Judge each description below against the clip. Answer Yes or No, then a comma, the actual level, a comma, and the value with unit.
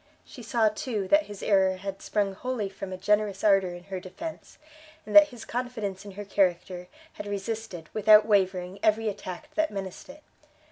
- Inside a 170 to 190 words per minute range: Yes, average, 180 wpm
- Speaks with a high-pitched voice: Yes, high, 205 Hz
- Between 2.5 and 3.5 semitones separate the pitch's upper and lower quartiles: Yes, average, 2.8 semitones